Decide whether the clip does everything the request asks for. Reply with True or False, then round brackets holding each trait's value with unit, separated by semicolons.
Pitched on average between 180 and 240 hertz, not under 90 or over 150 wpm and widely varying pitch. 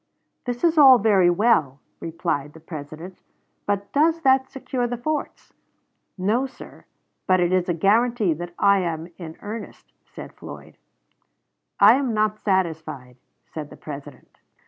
True (190 Hz; 145 wpm; 7.0 semitones)